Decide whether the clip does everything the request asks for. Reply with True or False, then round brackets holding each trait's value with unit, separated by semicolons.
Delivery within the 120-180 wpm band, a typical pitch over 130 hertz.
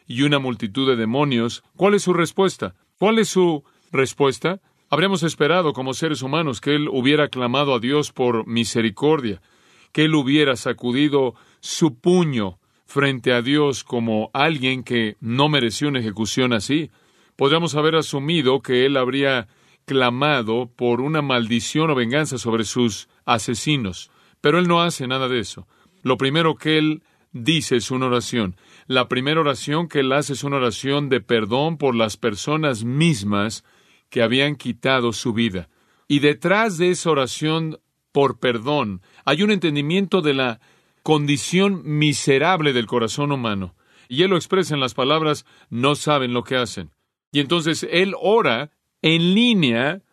True (155 wpm; 140 Hz)